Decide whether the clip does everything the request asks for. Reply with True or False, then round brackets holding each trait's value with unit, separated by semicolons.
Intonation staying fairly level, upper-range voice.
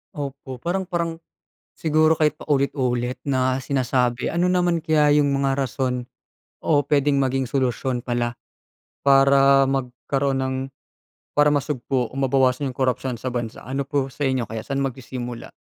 False (2.2 semitones; 135 Hz)